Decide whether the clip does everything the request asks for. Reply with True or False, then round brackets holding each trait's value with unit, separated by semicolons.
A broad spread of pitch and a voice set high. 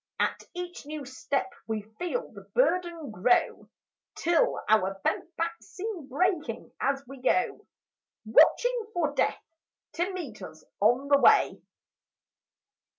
True (6.4 semitones; 285 Hz)